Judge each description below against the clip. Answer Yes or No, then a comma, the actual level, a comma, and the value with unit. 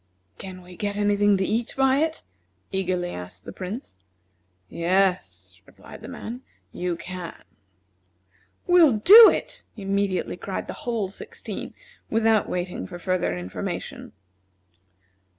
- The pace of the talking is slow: Yes, slow, 125 wpm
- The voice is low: No, high, 190 Hz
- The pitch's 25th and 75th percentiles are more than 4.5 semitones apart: No, average, 3.8 semitones